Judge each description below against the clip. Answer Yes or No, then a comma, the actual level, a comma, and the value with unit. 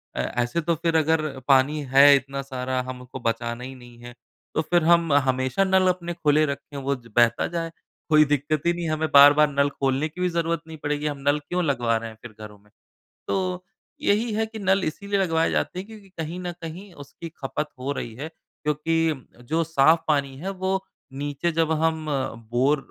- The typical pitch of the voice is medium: Yes, medium, 150 Hz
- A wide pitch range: No, average, 4.0 semitones